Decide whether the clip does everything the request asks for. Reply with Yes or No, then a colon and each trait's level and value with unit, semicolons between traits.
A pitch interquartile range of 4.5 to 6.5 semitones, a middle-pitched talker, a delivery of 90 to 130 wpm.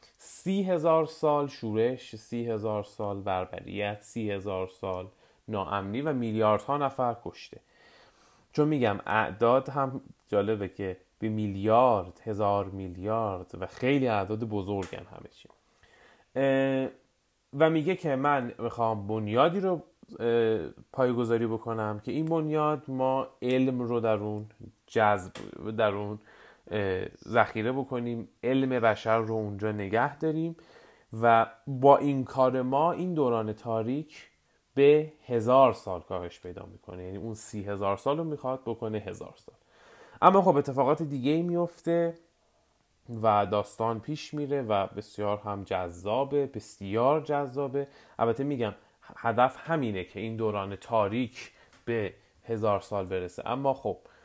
No: average, 4.9 semitones; low, 115 Hz; average, 125 wpm